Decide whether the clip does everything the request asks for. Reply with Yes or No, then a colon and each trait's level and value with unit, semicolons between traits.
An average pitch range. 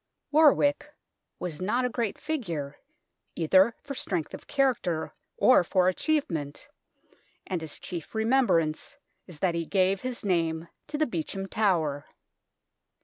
No: wide, 7.4 semitones